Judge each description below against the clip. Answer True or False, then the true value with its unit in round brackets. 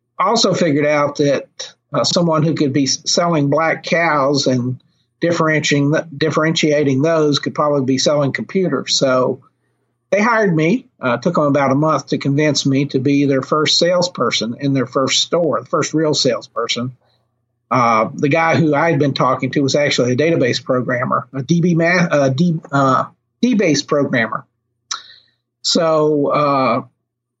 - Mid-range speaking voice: True (145 Hz)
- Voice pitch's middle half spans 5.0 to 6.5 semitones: False (3.2 semitones)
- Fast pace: False (155 wpm)